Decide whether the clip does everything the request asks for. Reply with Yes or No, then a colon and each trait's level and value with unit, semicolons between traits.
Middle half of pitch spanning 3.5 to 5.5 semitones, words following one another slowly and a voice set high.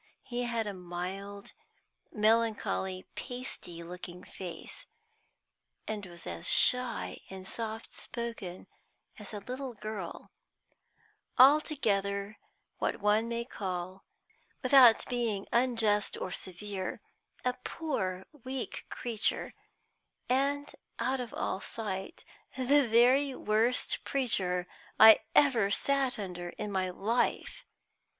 Yes: average, 4.6 semitones; slow, 105 wpm; high, 220 Hz